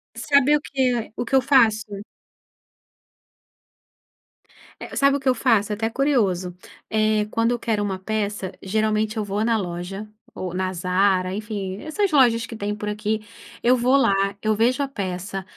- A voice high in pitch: Yes, high, 215 Hz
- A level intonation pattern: No, average, 3.6 semitones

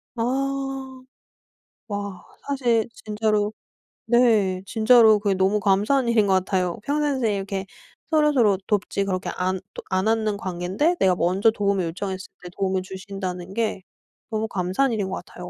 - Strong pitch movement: No, average, 3.6 semitones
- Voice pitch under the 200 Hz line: No, high, 205 Hz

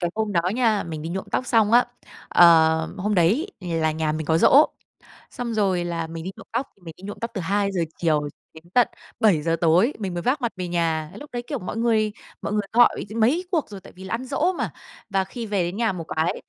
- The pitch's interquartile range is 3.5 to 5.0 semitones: No, wide, 5.5 semitones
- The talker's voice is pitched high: Yes, high, 195 Hz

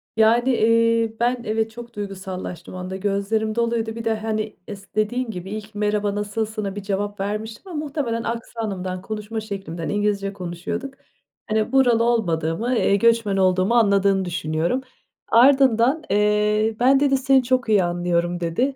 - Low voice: No, high, 215 Hz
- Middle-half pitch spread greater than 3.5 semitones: No, average, 2.9 semitones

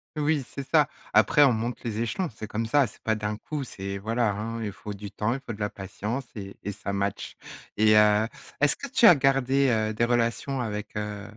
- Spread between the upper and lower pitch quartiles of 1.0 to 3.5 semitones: No, average, 4.3 semitones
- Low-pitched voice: Yes, low, 110 Hz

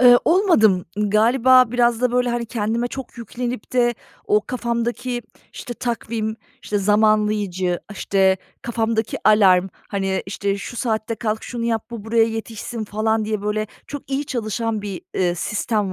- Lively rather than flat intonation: No, narrow, 2.5 semitones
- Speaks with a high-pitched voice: Yes, high, 225 Hz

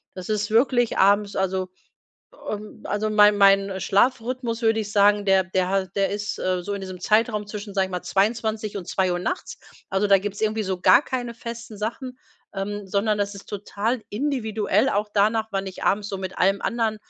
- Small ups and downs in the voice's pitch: Yes, narrow, 2.3 semitones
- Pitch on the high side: Yes, high, 205 Hz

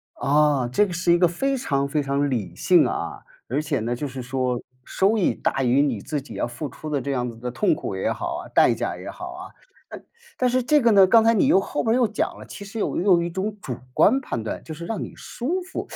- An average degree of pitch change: No, wide, 8.1 semitones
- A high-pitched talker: No, medium, 155 Hz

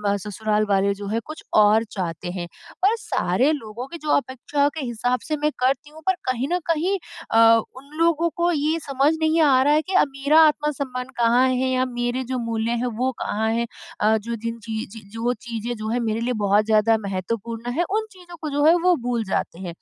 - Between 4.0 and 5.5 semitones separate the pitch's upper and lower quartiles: Yes, average, 5.1 semitones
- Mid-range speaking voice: No, high, 245 Hz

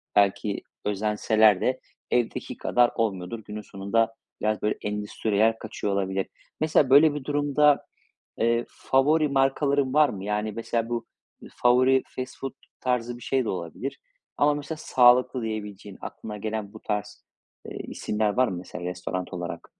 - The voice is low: Yes, low, 115 Hz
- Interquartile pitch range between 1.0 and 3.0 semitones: No, average, 4.1 semitones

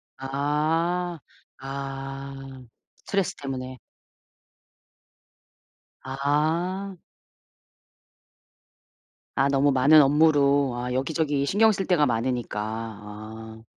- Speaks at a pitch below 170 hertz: Yes, medium, 140 Hz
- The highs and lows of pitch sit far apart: No, average, 3.4 semitones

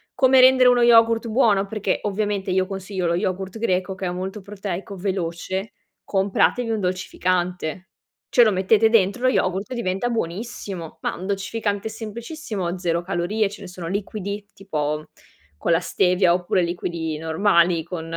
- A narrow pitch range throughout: No, average, 3.3 semitones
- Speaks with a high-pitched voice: Yes, high, 195 Hz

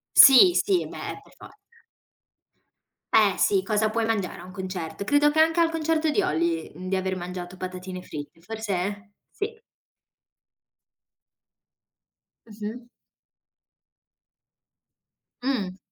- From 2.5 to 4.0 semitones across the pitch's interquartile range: No, wide, 8.1 semitones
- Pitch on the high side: Yes, high, 205 Hz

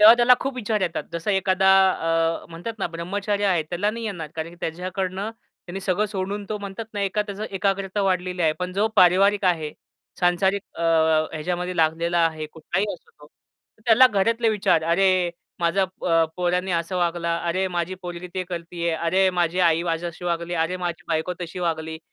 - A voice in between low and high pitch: Yes, medium, 180 Hz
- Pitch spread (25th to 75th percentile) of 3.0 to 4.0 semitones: No, narrow, 2.6 semitones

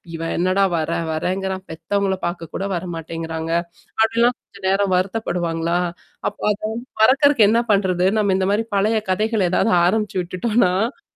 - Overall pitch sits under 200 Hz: Yes, high, 190 Hz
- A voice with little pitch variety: No, average, 3.7 semitones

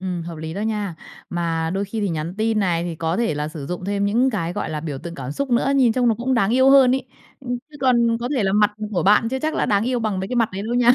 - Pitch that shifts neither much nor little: No, wide, 5.8 semitones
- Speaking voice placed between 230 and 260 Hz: No, high, 205 Hz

